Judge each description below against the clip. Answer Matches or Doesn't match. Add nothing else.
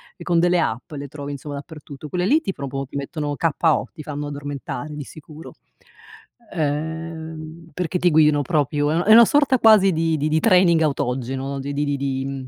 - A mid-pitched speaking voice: Matches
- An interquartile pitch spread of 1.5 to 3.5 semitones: Matches